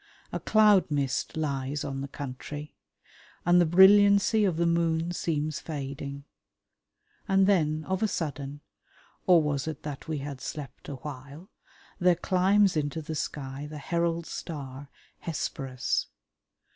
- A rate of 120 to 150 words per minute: Yes, slow, 135 wpm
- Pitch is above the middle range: No, medium, 155 Hz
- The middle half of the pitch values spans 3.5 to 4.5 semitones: Yes, average, 3.8 semitones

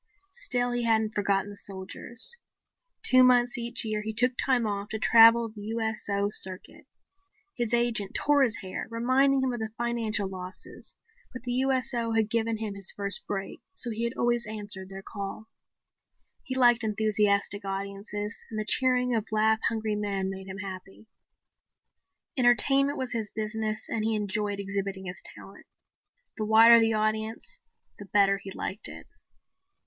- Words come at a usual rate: Yes, average, 160 wpm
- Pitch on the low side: No, high, 220 Hz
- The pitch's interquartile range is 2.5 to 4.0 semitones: Yes, average, 2.9 semitones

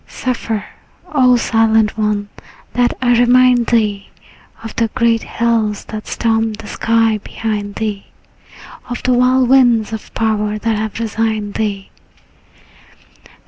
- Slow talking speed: Yes, slow, 125 wpm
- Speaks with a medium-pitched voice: No, high, 225 Hz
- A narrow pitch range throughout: Yes, narrow, 2.1 semitones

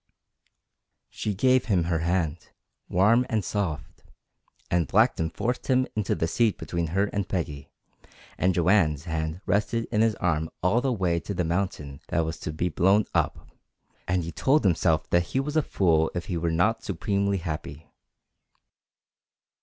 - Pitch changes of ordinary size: Yes, average, 4.2 semitones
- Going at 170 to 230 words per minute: No, average, 160 wpm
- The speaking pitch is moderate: No, very low, 90 Hz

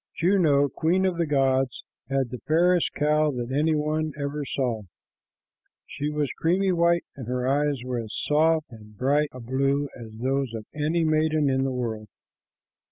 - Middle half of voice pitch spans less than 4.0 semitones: Yes, average, 3.4 semitones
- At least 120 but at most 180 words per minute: Yes, average, 170 wpm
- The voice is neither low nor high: Yes, medium, 145 Hz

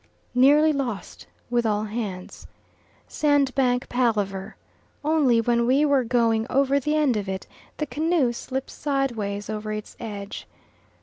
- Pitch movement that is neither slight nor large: Yes, average, 4.5 semitones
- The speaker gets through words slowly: Yes, slow, 130 wpm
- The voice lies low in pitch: No, high, 245 Hz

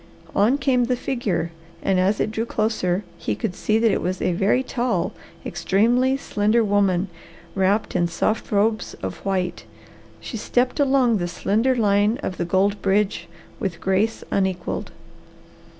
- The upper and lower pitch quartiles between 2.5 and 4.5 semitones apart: Yes, average, 3.7 semitones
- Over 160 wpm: No, average, 150 wpm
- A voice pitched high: Yes, high, 205 Hz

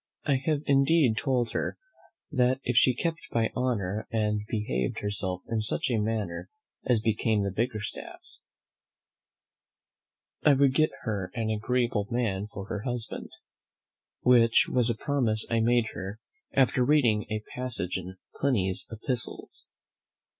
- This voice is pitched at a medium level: No, low, 115 Hz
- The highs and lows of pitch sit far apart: No, average, 3.2 semitones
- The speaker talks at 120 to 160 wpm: Yes, slow, 135 wpm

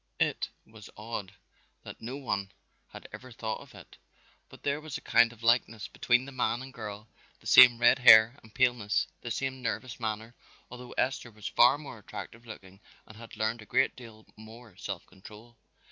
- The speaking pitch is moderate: No, low, 115 Hz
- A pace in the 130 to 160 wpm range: No, average, 185 wpm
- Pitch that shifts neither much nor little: No, narrow, 2.3 semitones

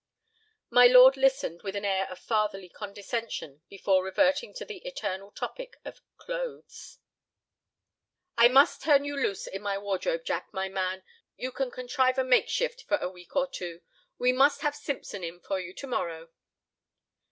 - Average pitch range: No, wide, 6.3 semitones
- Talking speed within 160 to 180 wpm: Yes, average, 165 wpm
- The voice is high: Yes, high, 235 Hz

